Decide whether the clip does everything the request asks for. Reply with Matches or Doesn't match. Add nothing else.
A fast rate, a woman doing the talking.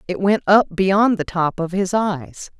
Matches